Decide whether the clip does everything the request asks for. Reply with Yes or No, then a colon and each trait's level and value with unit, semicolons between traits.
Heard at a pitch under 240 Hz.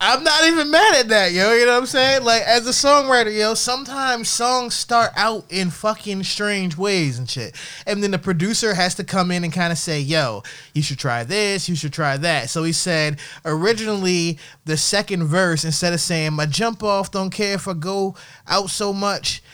Yes: high, 190 Hz